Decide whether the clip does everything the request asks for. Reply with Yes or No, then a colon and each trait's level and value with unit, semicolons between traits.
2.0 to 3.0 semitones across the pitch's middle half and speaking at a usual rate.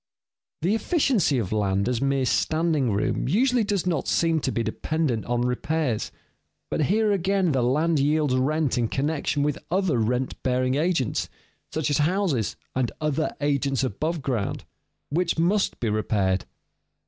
No: average, 5.0 semitones; average, 150 wpm